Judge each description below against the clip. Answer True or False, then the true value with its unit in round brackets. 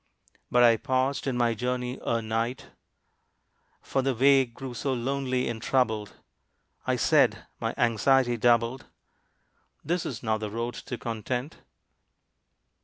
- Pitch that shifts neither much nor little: False (2.3 semitones)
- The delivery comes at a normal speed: False (130 wpm)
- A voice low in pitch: True (125 Hz)